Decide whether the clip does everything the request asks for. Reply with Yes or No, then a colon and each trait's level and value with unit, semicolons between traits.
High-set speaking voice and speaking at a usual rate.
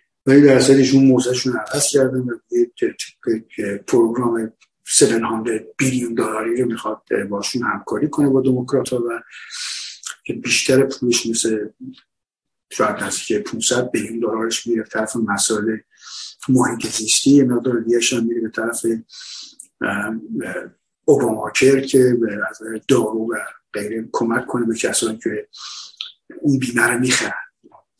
No: low, 120 Hz; average, 125 wpm